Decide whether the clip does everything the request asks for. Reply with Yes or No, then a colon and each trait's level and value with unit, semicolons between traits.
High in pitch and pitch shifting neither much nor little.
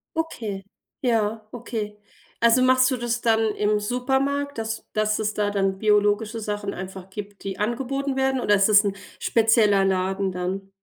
Yes: high, 215 Hz; average, 3.0 semitones